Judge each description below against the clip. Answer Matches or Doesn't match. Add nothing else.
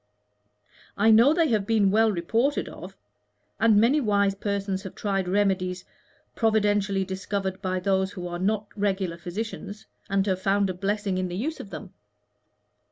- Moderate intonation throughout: Doesn't match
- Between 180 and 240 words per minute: Doesn't match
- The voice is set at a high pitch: Matches